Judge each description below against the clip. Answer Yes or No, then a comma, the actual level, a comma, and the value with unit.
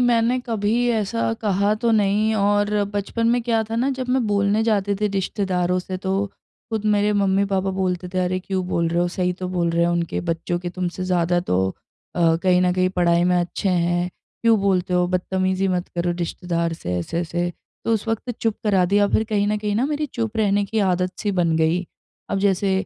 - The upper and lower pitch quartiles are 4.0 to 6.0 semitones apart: No, average, 3.0 semitones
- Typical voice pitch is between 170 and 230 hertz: Yes, high, 190 Hz